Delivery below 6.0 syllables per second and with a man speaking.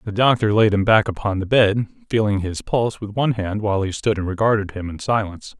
No: 6.1 syllables/s; male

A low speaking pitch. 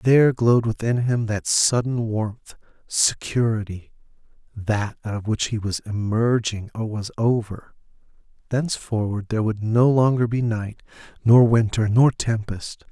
Yes: low, 110 Hz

